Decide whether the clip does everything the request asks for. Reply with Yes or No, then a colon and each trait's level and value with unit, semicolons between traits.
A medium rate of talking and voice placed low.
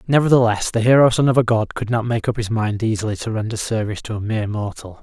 No: fast, 250 wpm; low, 115 Hz